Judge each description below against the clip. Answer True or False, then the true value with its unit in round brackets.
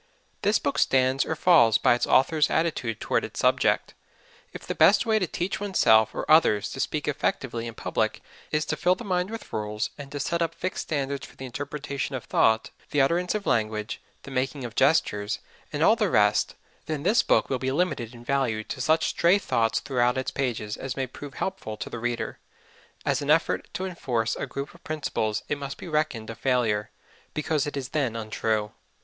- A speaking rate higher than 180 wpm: True (205 wpm)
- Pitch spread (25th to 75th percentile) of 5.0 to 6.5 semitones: True (5.4 semitones)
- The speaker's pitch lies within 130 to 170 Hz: True (135 Hz)